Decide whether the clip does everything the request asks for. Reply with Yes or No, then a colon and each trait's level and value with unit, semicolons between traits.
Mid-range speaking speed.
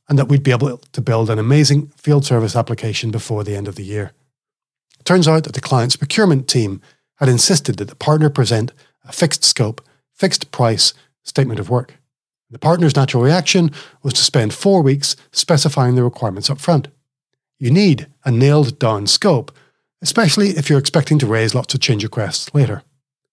Yes: average, 185 wpm